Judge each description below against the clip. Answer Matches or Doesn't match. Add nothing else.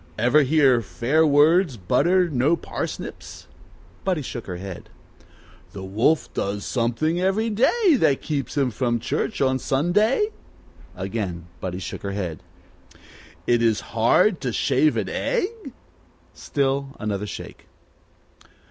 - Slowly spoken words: Matches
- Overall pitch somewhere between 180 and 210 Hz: Doesn't match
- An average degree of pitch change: Doesn't match